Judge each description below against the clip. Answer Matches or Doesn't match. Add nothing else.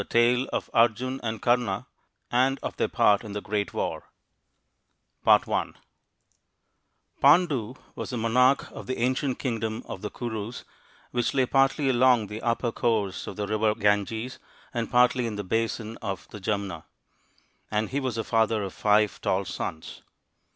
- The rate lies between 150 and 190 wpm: Matches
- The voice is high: Doesn't match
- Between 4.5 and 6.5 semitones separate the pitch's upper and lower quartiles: Doesn't match